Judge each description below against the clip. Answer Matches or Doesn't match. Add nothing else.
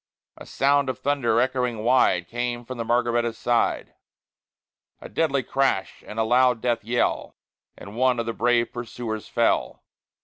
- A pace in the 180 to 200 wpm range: Doesn't match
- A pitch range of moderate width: Doesn't match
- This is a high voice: Doesn't match